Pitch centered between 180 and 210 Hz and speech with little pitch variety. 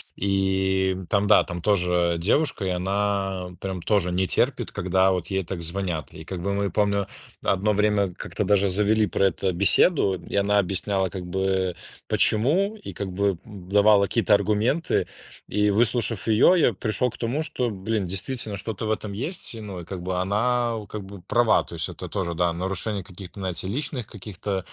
No: low, 100 Hz; narrow, 2.3 semitones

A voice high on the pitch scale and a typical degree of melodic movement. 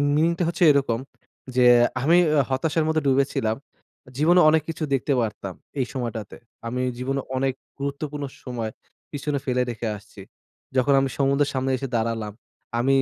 No: low, 135 Hz; average, 3.4 semitones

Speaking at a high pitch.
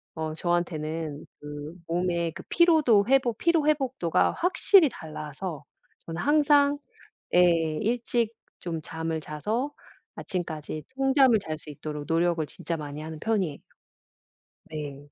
No: medium, 170 Hz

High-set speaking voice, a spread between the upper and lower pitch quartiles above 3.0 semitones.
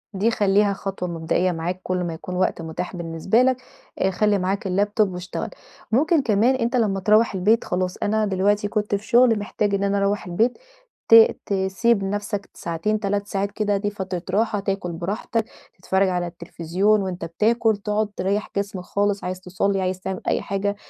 No: high, 200 Hz; narrow, 2.4 semitones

